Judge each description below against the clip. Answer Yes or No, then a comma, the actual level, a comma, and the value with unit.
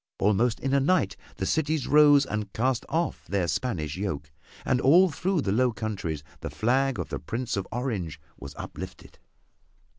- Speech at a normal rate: Yes, average, 170 wpm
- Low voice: Yes, low, 120 Hz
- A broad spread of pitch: Yes, wide, 6.0 semitones